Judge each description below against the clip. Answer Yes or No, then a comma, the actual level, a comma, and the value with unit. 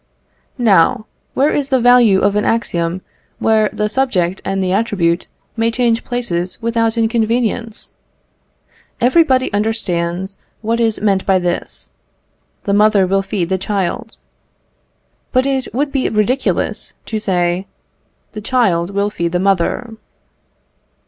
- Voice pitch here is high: Yes, high, 215 Hz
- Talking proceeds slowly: Yes, slow, 130 wpm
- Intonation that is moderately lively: Yes, average, 3.7 semitones